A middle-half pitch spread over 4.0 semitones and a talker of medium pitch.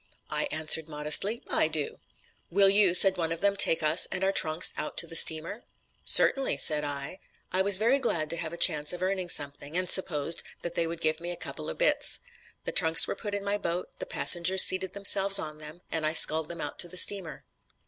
No: average, 3.7 semitones; medium, 175 Hz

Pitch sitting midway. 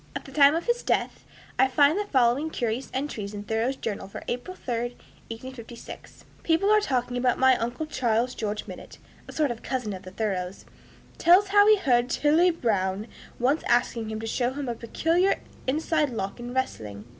No: very high, 250 Hz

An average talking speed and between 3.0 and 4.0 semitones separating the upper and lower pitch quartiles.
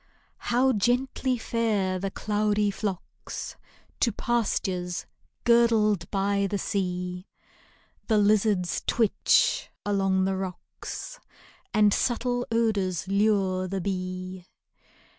No: slow, 95 wpm; average, 3.3 semitones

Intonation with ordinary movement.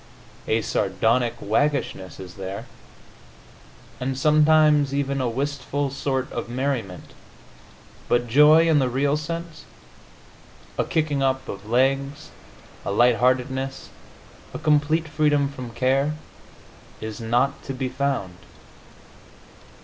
Yes: average, 3.2 semitones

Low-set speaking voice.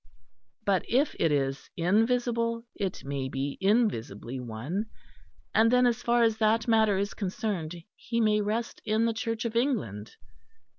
No: high, 215 Hz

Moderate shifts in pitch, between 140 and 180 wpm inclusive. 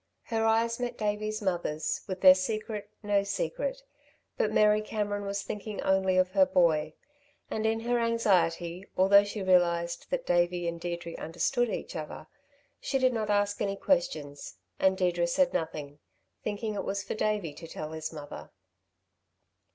Yes: average, 3.9 semitones; average, 160 wpm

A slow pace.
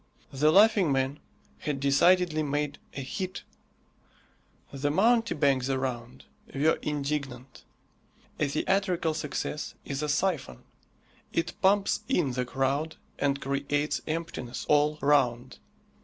Yes: slow, 110 wpm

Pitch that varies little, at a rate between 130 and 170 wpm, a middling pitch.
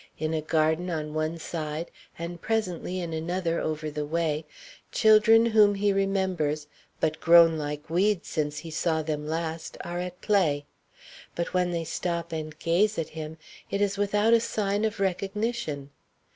No: average, 3.9 semitones; average, 160 wpm; medium, 170 Hz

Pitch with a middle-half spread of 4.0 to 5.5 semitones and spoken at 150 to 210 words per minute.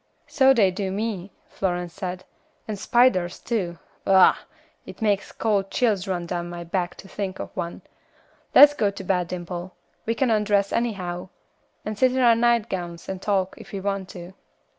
No: average, 3.3 semitones; average, 170 wpm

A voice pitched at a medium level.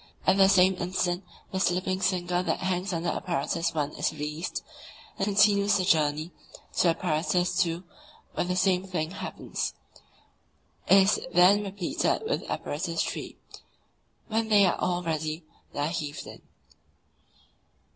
Yes: medium, 180 Hz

